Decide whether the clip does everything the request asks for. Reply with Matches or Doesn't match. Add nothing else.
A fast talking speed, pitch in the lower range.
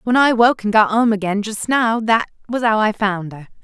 Doesn't match